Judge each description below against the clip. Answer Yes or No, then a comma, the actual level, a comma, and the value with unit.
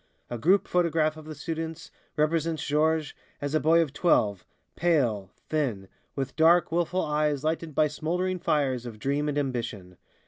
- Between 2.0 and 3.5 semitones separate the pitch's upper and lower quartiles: Yes, average, 3.2 semitones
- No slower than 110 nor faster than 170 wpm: Yes, average, 160 wpm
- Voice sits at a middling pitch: Yes, medium, 155 Hz